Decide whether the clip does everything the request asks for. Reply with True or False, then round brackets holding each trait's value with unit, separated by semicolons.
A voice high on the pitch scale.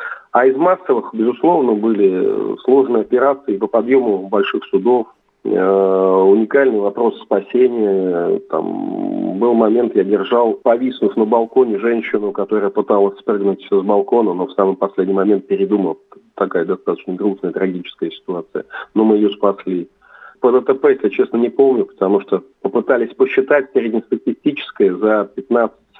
False (110 Hz)